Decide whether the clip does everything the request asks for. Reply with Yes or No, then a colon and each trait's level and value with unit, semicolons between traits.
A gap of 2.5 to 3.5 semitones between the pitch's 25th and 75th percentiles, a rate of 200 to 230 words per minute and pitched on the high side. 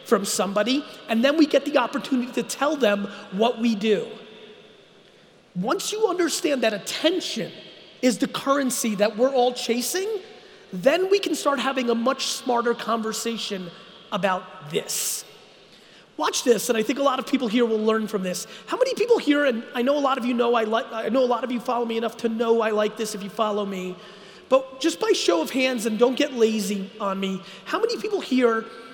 No: average, 4.1 semitones; fast, 205 wpm; high, 240 Hz